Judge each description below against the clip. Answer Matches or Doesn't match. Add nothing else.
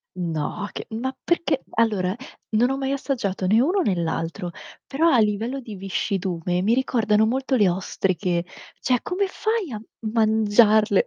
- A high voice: Matches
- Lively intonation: Matches